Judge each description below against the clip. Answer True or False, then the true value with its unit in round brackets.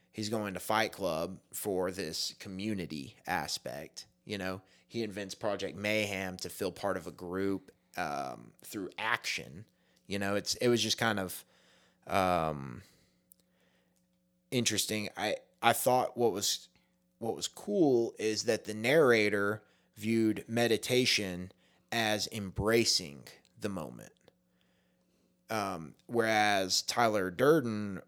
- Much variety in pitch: False (3.5 semitones)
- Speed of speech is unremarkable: False (120 wpm)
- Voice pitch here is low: True (100 Hz)